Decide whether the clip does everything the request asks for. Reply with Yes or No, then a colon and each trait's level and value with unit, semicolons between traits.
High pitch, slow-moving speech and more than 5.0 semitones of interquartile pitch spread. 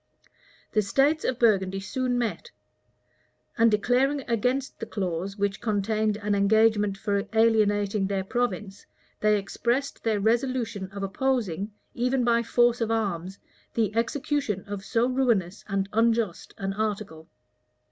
No: high, 215 Hz; slow, 130 wpm; average, 3.2 semitones